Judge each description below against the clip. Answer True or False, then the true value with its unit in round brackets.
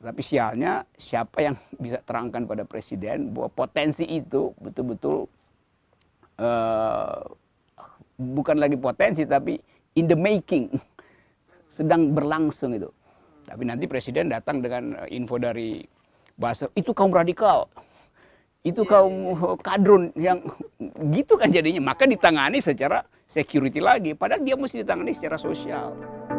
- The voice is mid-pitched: True (155 Hz)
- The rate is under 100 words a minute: False (120 wpm)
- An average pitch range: False (6.3 semitones)